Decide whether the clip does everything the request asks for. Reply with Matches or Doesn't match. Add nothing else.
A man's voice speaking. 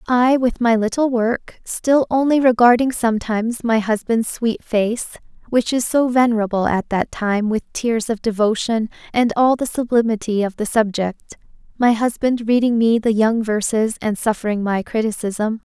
Doesn't match